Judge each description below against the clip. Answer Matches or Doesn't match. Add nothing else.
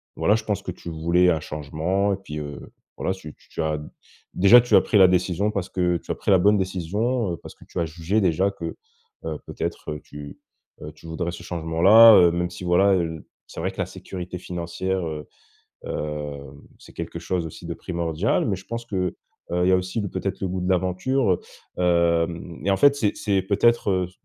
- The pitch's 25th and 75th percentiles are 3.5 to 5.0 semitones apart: Doesn't match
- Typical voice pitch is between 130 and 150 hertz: Doesn't match